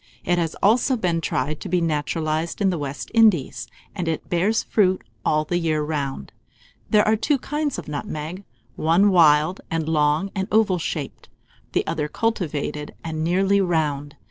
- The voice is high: No, medium, 165 Hz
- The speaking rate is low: No, average, 165 wpm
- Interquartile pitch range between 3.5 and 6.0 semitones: Yes, average, 4.3 semitones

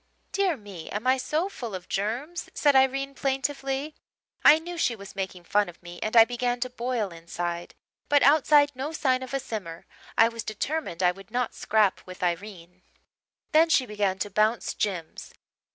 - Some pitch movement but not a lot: No, wide, 6.0 semitones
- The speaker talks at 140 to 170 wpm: No, average, 180 wpm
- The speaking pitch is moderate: No, high, 230 Hz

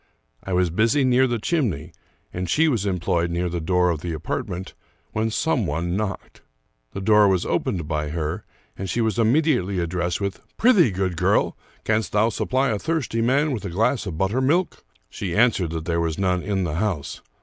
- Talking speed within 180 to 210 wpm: Yes, average, 195 wpm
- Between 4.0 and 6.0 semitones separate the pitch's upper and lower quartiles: Yes, average, 5.1 semitones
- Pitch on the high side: No, very low, 95 Hz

